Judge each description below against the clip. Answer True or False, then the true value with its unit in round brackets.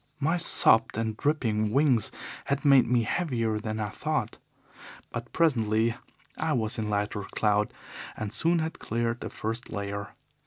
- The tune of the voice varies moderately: True (4.0 semitones)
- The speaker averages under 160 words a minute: True (150 wpm)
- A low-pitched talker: True (115 Hz)